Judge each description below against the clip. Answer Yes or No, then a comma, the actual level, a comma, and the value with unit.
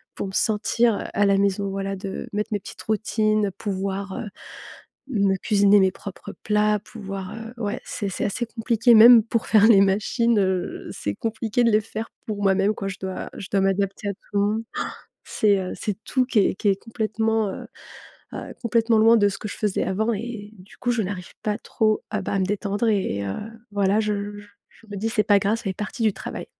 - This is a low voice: No, high, 210 Hz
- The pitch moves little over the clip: Yes, narrow, 2.2 semitones